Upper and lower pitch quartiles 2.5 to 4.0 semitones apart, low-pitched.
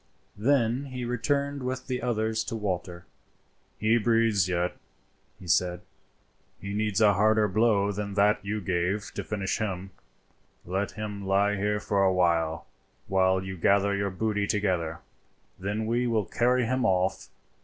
Yes: average, 3.0 semitones; low, 105 Hz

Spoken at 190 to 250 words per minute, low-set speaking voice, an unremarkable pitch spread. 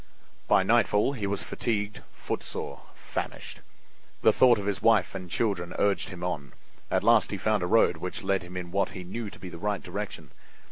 Yes: average, 195 wpm; low, 100 Hz; average, 3.0 semitones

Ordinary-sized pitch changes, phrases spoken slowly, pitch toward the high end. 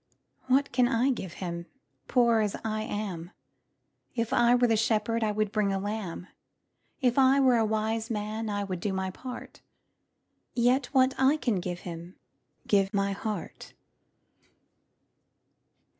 No: average, 3.6 semitones; average, 150 wpm; high, 215 Hz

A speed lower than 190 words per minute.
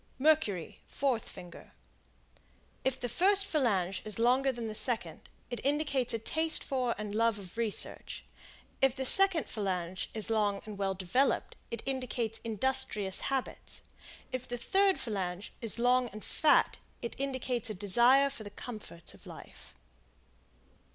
Yes: average, 145 wpm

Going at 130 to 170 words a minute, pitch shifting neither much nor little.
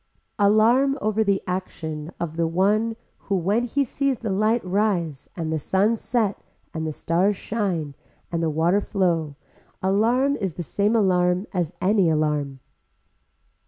Yes: average, 150 wpm; average, 4.6 semitones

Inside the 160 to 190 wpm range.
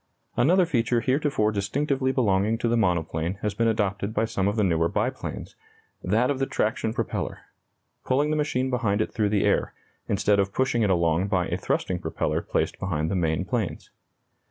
Yes: average, 180 wpm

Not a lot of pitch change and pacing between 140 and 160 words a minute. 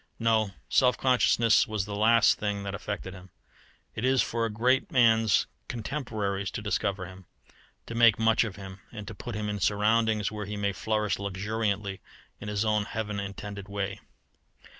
No: narrow, 2.0 semitones; average, 170 wpm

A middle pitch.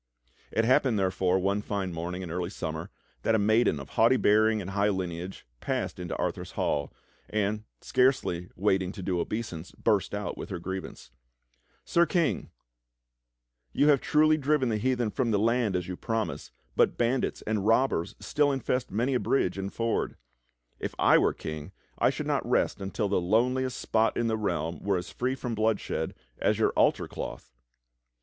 No: low, 105 Hz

